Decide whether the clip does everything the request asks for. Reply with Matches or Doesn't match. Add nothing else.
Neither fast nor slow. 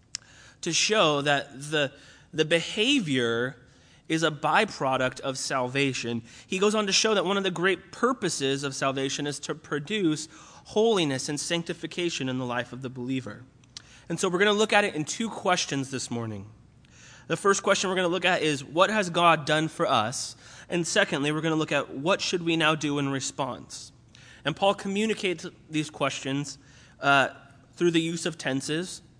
Matches